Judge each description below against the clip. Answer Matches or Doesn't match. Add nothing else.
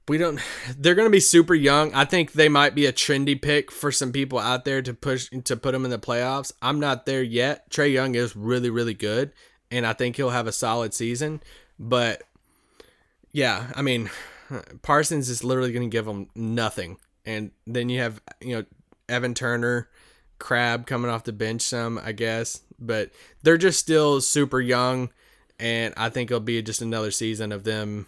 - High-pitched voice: Doesn't match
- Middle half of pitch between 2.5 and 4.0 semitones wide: Matches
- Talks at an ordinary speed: Matches